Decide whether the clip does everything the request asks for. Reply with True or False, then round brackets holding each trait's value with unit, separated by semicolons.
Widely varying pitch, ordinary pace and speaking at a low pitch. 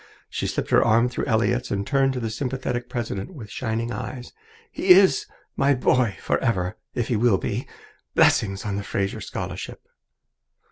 False (3.4 semitones; 160 wpm; 120 Hz)